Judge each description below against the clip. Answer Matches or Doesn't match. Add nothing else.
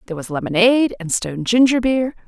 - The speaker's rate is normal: Matches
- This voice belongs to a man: Doesn't match